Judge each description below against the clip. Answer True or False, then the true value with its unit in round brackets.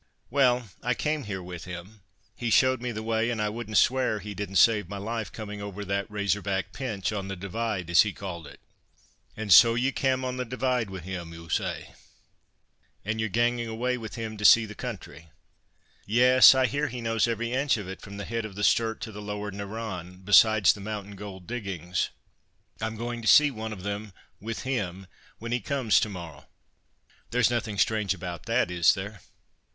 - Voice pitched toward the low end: True (110 Hz)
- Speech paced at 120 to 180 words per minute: False (200 wpm)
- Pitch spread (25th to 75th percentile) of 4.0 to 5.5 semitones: False (3.3 semitones)